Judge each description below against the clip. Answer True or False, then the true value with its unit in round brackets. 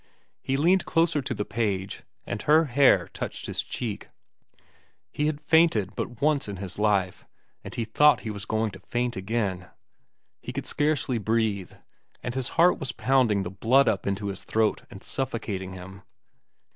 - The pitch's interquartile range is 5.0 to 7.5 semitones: True (5.4 semitones)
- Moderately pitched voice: False (110 Hz)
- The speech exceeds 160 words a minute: True (170 wpm)